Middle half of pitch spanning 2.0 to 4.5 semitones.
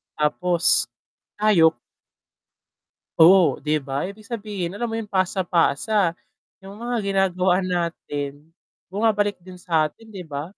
Yes: average, 3.9 semitones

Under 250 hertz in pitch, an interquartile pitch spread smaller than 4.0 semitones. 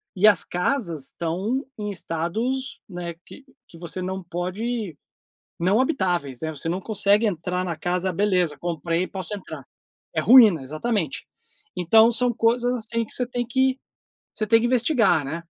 No: high, 190 Hz; average, 5.3 semitones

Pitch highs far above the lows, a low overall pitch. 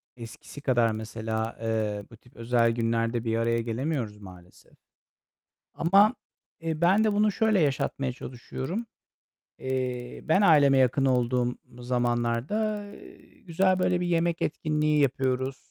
Yes: wide, 5.9 semitones; low, 130 Hz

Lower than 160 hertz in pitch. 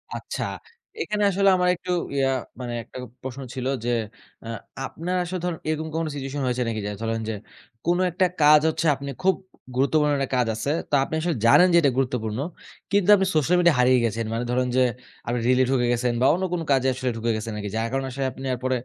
Yes: low, 135 Hz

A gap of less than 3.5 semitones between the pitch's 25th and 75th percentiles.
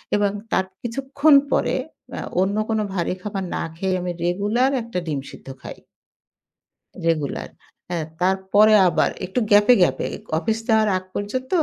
No: average, 3.8 semitones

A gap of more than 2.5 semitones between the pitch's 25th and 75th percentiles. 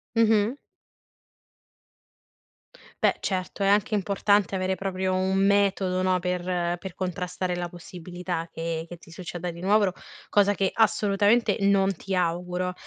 No: narrow, 1.9 semitones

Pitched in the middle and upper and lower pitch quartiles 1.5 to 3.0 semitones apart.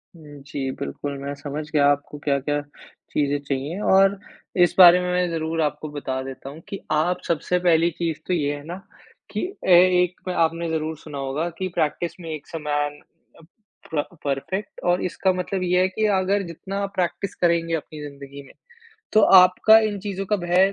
No: medium, 165 Hz; average, 3.7 semitones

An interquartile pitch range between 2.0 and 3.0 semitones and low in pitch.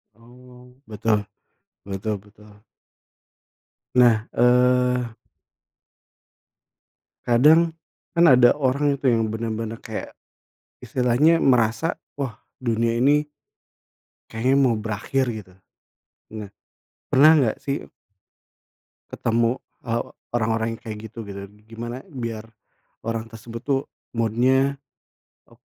Yes: narrow, 2.6 semitones; low, 120 Hz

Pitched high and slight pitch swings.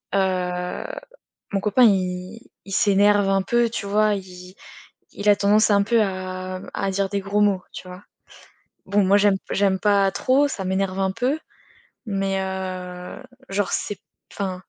Yes: high, 195 Hz; narrow, 1.7 semitones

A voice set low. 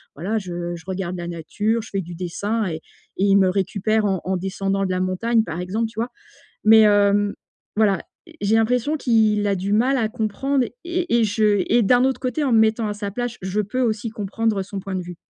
No: high, 205 Hz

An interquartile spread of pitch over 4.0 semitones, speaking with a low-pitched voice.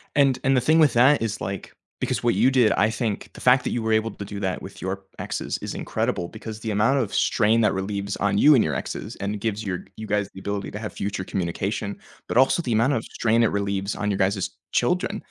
No: average, 2.8 semitones; low, 105 Hz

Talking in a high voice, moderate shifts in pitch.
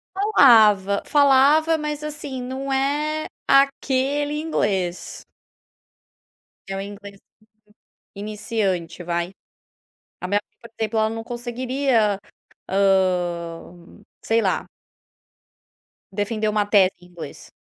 No: high, 220 Hz; wide, 6.0 semitones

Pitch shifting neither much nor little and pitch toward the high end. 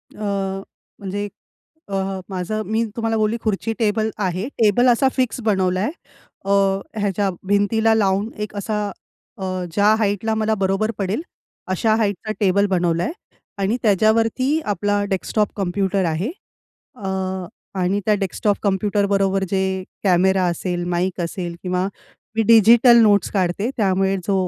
No: narrow, 2.3 semitones; high, 200 Hz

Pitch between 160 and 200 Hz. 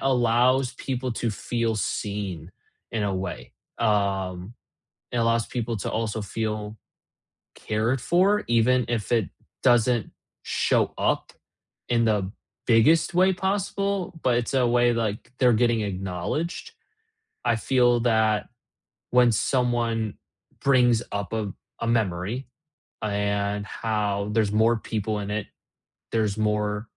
No: low, 115 Hz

